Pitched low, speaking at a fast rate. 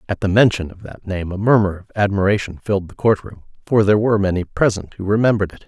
Yes: low, 100 Hz; fast, 235 wpm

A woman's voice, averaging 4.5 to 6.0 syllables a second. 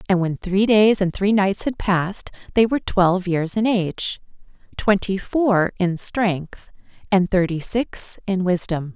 No: female; 4.2 syllables/s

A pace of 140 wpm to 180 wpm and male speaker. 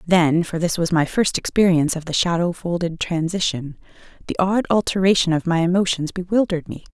No: average, 170 wpm; female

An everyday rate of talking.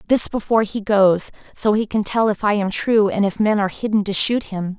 No: fast, 250 wpm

